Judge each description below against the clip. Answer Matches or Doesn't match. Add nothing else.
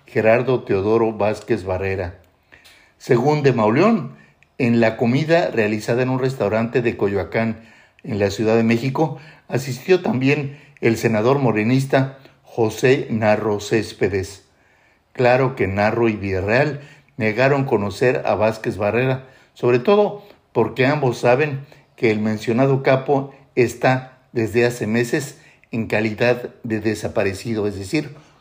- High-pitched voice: Doesn't match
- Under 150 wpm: Matches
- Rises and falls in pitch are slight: Doesn't match